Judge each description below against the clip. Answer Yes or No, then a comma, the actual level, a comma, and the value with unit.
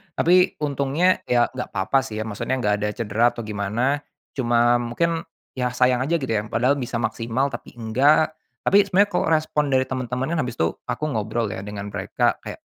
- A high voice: No, low, 125 Hz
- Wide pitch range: No, average, 4.0 semitones